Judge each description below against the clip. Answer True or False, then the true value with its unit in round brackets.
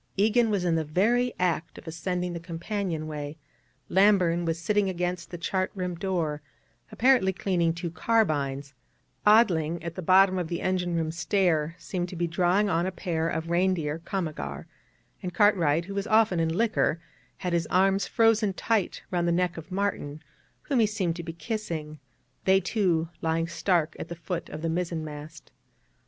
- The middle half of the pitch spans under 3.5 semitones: True (2.9 semitones)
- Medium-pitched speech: True (175 Hz)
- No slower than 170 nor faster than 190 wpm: True (175 wpm)